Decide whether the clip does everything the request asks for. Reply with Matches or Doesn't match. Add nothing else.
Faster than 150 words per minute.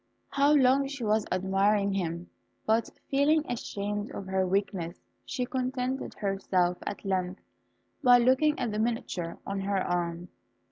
Doesn't match